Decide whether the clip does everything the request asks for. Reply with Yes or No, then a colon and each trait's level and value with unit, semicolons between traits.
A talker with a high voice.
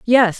Yes: high, 225 Hz